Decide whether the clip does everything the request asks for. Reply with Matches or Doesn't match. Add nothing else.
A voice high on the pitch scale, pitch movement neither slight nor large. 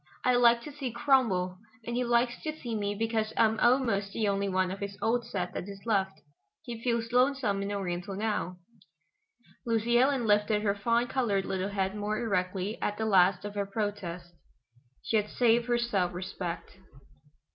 Matches